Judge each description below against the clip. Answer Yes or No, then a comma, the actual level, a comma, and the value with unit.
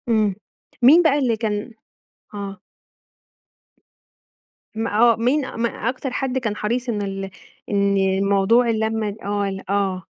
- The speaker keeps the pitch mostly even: No, average, 3.2 semitones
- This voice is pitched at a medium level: No, high, 220 Hz